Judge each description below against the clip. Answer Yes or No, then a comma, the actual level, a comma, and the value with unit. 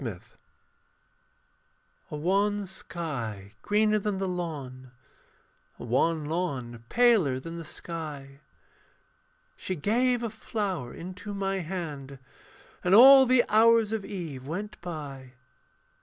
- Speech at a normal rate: No, slow, 110 wpm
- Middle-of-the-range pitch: Yes, medium, 175 Hz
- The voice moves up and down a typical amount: No, wide, 6.9 semitones